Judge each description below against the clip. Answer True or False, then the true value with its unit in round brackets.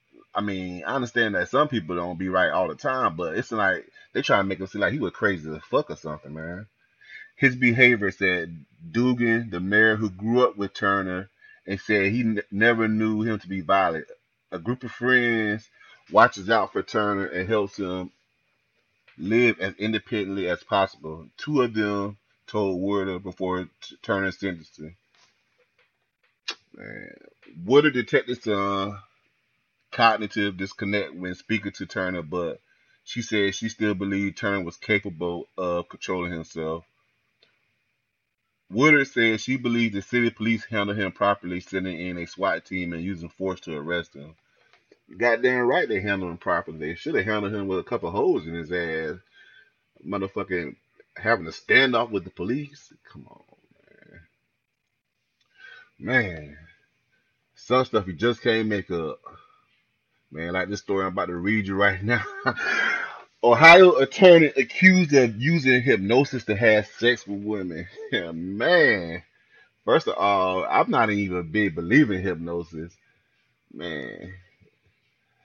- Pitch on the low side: True (100 Hz)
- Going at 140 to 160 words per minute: True (155 wpm)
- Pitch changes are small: False (4.1 semitones)